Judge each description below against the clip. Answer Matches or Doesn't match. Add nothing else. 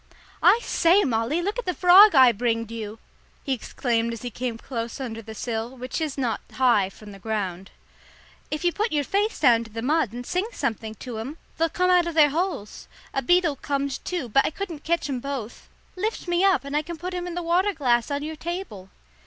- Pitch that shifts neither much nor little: Doesn't match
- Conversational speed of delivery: Doesn't match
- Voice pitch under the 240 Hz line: Doesn't match